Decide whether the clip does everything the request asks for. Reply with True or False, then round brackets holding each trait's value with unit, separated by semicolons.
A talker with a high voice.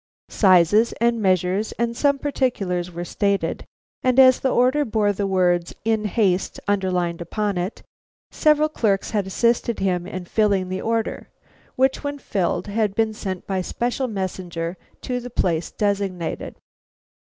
True (205 Hz)